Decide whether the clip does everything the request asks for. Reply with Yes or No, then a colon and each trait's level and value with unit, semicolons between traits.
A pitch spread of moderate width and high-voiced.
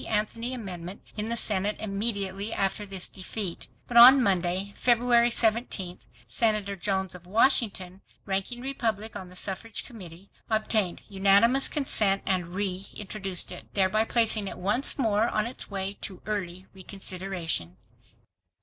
Yes: average, 3.0 semitones; high, 200 Hz